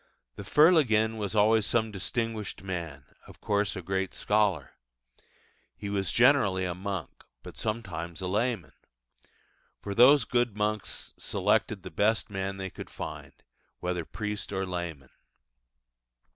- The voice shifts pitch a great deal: No, average, 3.1 semitones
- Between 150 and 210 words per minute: No, slow, 135 wpm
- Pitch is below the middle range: Yes, low, 100 Hz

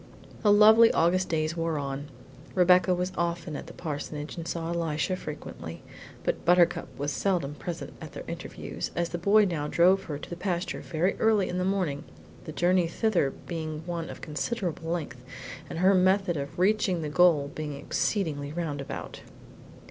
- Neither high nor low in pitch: Yes, medium, 170 Hz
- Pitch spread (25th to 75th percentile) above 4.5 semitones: No, average, 3.3 semitones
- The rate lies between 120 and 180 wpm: Yes, average, 170 wpm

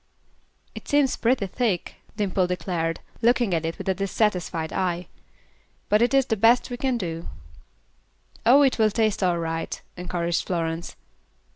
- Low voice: No, high, 190 Hz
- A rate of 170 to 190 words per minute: No, average, 150 wpm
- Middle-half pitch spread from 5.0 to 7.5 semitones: Yes, wide, 5.4 semitones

